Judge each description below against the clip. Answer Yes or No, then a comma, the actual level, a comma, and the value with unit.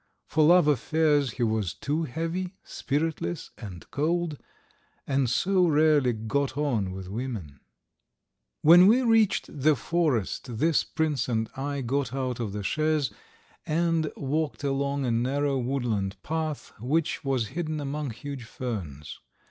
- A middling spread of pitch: Yes, average, 4.7 semitones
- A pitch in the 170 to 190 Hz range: No, medium, 140 Hz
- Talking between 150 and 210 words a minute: No, slow, 135 wpm